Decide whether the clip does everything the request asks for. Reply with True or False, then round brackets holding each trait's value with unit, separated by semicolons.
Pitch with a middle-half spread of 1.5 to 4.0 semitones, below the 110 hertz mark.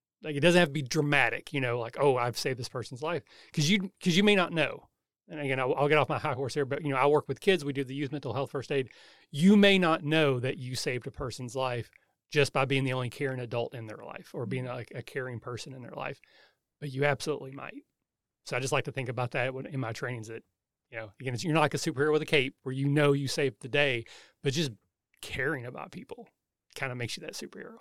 False (2.9 semitones; 140 Hz)